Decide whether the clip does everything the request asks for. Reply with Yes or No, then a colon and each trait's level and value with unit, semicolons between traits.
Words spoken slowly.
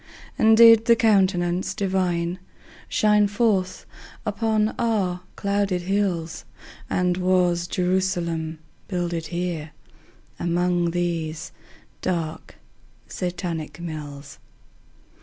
Yes: slow, 85 wpm